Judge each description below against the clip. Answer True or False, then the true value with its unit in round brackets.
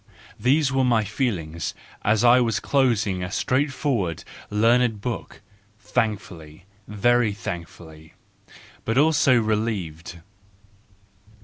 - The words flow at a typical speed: False (95 wpm)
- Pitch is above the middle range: False (110 Hz)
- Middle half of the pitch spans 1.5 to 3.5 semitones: False (5.2 semitones)